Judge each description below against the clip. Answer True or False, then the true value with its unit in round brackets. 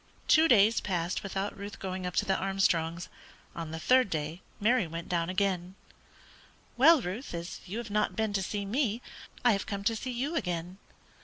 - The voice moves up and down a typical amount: True (4.1 semitones)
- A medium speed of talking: True (185 wpm)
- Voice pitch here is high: True (195 Hz)